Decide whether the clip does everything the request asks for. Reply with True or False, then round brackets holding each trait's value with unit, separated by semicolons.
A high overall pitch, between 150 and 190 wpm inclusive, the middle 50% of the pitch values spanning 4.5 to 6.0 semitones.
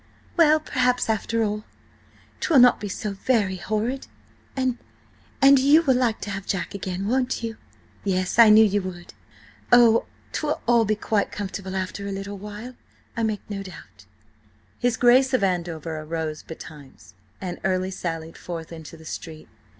True (205 Hz; 155 wpm; 4.8 semitones)